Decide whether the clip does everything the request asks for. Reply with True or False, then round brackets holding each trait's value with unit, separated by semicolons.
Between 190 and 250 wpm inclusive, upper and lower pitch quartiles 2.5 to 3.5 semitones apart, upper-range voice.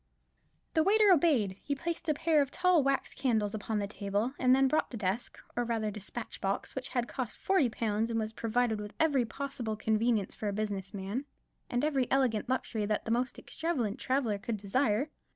False (195 wpm; 4.4 semitones; 235 Hz)